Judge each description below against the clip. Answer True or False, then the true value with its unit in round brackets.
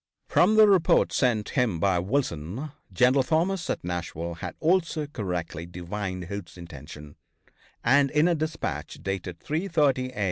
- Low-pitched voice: True (110 Hz)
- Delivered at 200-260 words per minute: False (145 wpm)